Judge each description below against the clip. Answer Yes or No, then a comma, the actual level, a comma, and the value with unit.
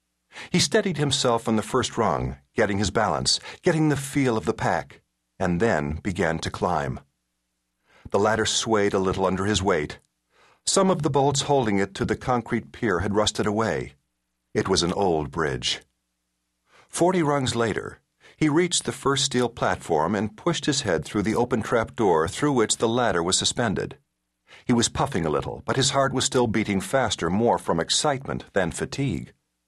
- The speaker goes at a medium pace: Yes, average, 180 wpm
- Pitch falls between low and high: No, low, 115 Hz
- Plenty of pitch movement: Yes, wide, 8.7 semitones